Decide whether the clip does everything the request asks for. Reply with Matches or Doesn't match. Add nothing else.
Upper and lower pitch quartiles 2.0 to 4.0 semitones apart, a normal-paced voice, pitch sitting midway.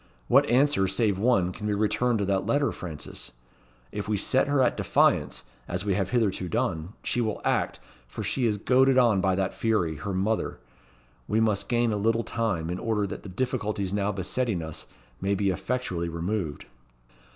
Doesn't match